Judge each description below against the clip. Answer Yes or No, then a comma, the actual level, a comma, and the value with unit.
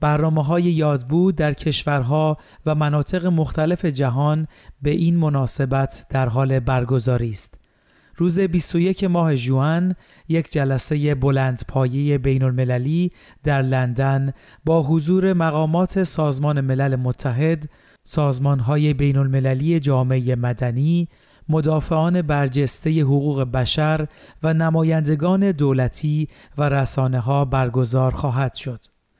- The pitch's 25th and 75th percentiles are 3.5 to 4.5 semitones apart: No, average, 3.1 semitones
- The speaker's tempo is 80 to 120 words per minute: Yes, average, 110 wpm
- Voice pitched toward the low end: No, medium, 145 Hz